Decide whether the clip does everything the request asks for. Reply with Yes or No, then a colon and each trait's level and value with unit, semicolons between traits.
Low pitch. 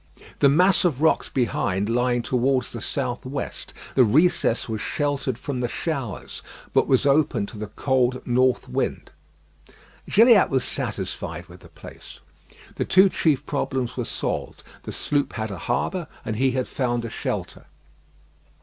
Yes: low, 130 Hz